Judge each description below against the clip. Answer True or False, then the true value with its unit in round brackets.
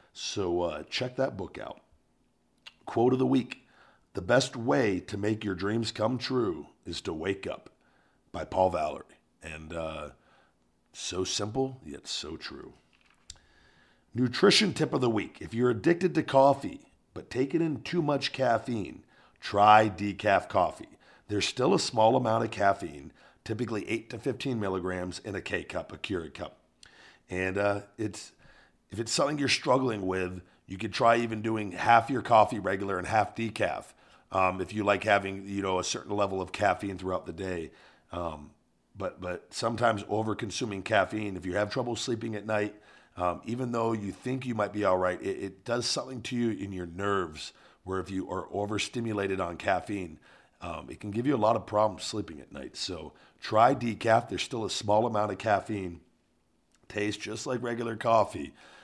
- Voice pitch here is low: True (105 Hz)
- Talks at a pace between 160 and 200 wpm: True (175 wpm)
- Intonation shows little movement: False (3.8 semitones)